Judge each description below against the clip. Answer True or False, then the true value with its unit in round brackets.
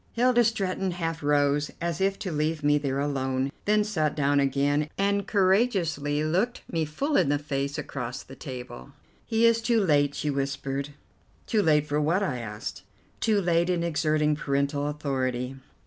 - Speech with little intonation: False (5.1 semitones)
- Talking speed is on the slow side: False (165 wpm)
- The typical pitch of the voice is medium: True (150 Hz)